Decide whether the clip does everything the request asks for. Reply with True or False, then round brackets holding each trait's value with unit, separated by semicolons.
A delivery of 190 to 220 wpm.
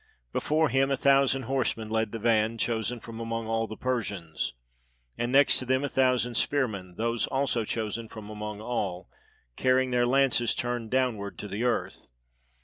False (165 wpm)